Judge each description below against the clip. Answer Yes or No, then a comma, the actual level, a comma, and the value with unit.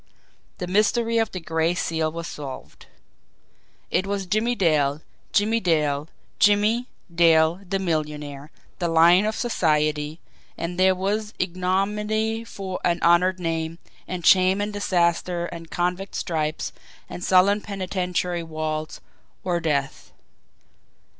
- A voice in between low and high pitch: Yes, medium, 180 Hz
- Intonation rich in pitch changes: No, average, 3.5 semitones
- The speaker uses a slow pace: Yes, slow, 120 wpm